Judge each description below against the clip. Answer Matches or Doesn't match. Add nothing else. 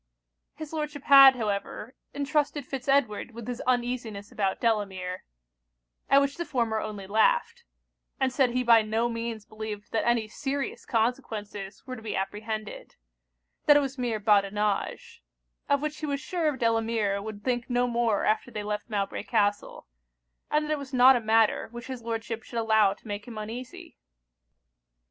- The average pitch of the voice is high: Matches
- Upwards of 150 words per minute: Matches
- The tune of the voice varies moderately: Matches